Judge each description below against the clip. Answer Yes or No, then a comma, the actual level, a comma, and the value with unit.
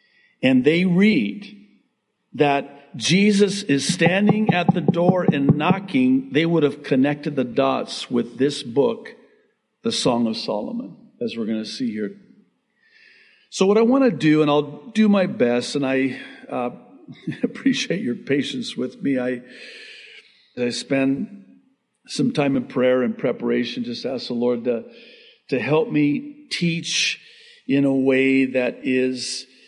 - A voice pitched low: No, medium, 170 Hz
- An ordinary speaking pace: Yes, average, 150 wpm